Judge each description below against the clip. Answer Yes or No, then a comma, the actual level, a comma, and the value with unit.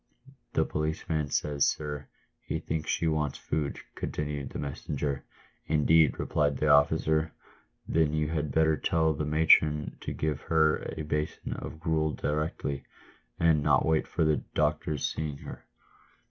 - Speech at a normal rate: Yes, average, 145 wpm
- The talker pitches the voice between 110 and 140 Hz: No, very low, 75 Hz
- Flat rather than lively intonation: Yes, narrow, 1.2 semitones